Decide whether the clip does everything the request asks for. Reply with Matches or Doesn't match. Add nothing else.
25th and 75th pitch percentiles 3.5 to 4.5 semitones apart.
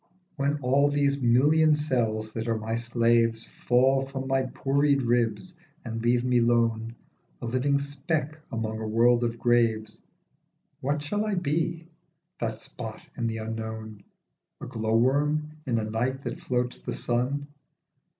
Matches